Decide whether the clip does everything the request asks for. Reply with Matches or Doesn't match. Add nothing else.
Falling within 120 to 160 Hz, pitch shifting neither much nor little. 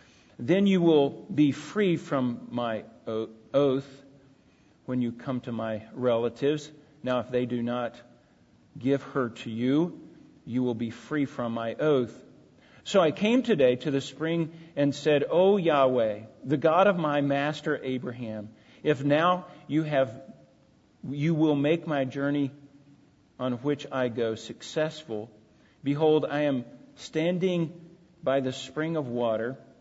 Matches